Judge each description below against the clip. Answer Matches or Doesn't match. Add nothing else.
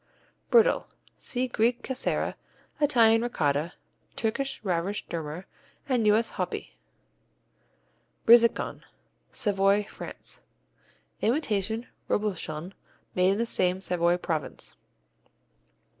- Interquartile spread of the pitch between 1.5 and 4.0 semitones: Doesn't match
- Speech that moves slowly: Matches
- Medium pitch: Doesn't match